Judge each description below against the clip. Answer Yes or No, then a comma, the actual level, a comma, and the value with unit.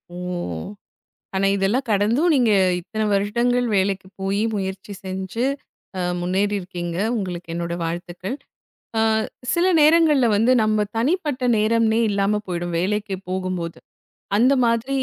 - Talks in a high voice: Yes, high, 205 Hz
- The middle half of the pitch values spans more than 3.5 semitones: Yes, average, 4.0 semitones